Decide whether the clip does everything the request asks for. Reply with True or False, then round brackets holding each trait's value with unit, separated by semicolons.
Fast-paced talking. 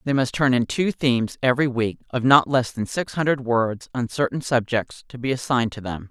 True (225 wpm)